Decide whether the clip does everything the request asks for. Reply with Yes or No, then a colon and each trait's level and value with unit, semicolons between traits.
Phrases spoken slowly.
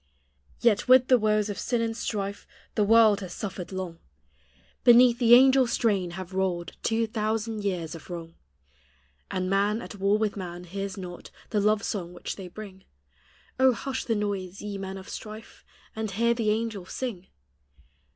No: average, 170 wpm